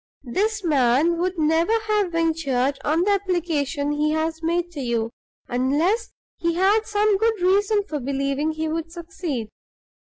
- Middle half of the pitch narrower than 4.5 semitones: No, average, 4.8 semitones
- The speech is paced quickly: No, average, 150 wpm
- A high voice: Yes, very high, 330 Hz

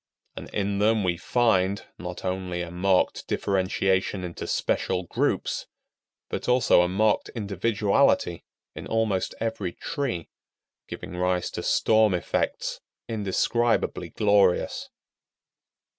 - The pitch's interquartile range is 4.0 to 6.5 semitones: No, average, 3.4 semitones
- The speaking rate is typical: No, slow, 110 wpm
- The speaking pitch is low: Yes, low, 100 Hz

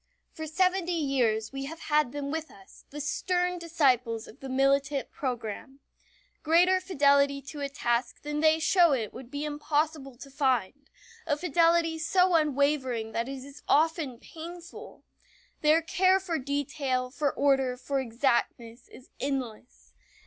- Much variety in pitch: No, average, 3.7 semitones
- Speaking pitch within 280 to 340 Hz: Yes, very high, 285 Hz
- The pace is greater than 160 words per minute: No, average, 145 wpm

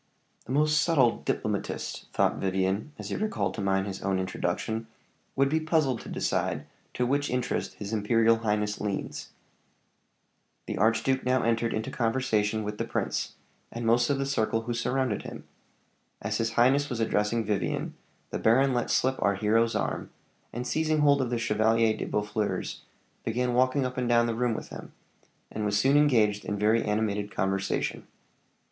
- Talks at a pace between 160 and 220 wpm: Yes, average, 170 wpm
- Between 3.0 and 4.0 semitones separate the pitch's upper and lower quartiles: Yes, average, 3.5 semitones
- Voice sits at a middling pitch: No, low, 115 Hz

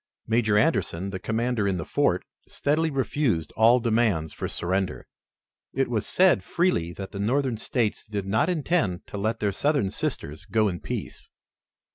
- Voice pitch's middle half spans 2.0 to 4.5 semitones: No, average, 5.2 semitones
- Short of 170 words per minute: Yes, average, 160 wpm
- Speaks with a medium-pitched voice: No, low, 110 Hz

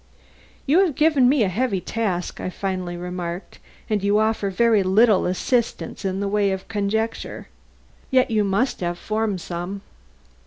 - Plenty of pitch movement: No, average, 3.5 semitones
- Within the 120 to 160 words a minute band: Yes, average, 155 wpm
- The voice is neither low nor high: No, high, 200 Hz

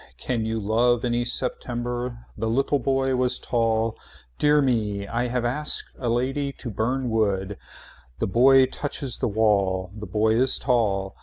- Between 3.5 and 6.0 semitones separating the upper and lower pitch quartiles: No, average, 2.7 semitones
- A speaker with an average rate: Yes, average, 155 wpm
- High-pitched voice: No, low, 120 Hz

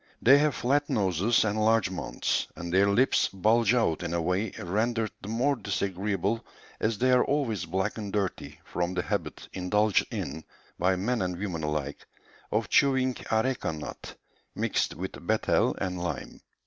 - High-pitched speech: No, low, 100 Hz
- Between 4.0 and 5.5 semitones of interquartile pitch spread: Yes, average, 4.5 semitones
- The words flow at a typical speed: Yes, average, 160 wpm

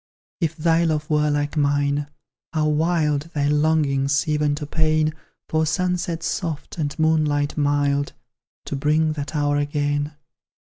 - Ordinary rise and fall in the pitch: No, narrow, 1.5 semitones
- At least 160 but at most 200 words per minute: No, slow, 135 wpm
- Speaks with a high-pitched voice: No, medium, 150 Hz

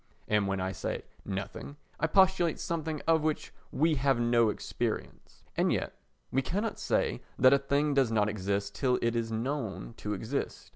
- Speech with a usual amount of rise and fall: No, wide, 6.1 semitones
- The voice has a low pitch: Yes, low, 130 Hz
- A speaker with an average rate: Yes, average, 175 wpm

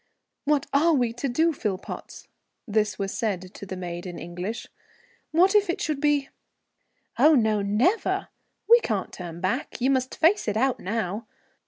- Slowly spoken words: No, average, 170 wpm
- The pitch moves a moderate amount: No, wide, 7.2 semitones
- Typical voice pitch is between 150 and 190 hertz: No, high, 230 Hz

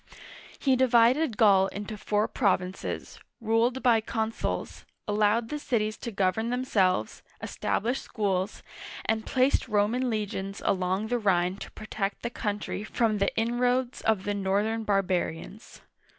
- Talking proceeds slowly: Yes, slow, 130 wpm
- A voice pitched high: Yes, high, 215 Hz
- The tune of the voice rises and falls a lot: No, average, 3.1 semitones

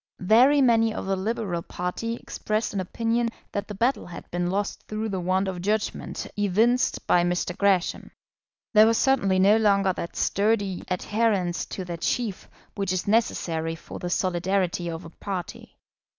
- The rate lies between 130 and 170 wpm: Yes, average, 165 wpm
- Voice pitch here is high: Yes, high, 195 Hz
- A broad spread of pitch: No, average, 3.6 semitones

